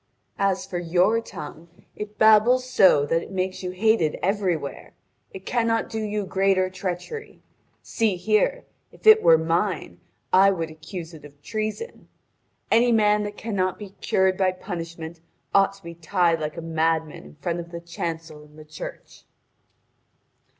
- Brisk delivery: No, average, 155 wpm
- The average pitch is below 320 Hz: Yes, medium, 185 Hz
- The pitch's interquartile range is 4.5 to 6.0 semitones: No, average, 4.1 semitones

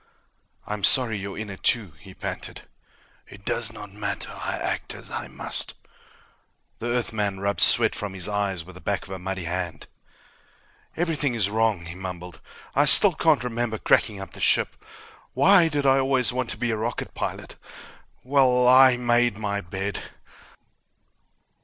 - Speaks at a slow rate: No, average, 165 wpm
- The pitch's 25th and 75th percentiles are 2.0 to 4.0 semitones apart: No, average, 4.4 semitones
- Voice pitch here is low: Yes, low, 110 Hz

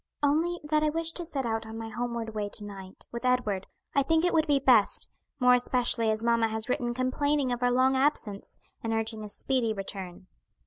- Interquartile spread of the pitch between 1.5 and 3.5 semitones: No, average, 4.0 semitones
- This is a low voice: No, high, 245 Hz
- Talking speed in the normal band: No, fast, 210 wpm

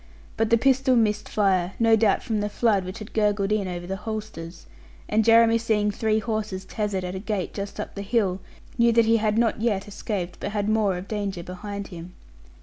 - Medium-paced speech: No, fast, 210 wpm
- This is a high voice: Yes, high, 210 Hz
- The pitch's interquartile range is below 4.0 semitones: Yes, narrow, 2.4 semitones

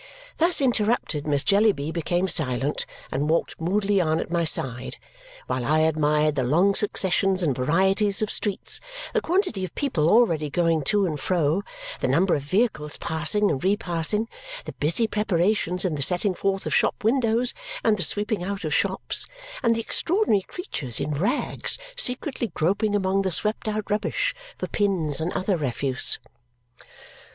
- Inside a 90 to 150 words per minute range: No, average, 160 wpm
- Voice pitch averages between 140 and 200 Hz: Yes, medium, 185 Hz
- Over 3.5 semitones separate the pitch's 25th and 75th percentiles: Yes, average, 5.3 semitones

